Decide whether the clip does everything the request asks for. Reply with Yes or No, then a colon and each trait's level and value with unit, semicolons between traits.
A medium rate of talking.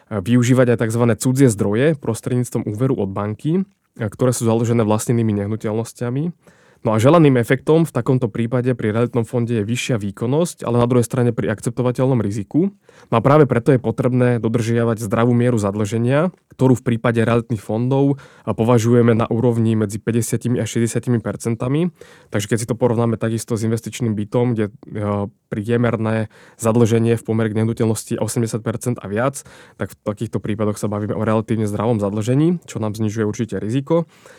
Yes: average, 155 wpm